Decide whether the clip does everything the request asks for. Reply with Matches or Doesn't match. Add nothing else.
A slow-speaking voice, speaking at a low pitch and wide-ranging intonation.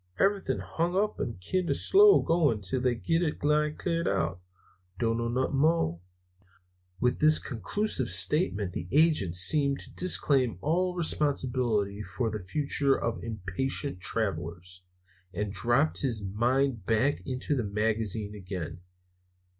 Matches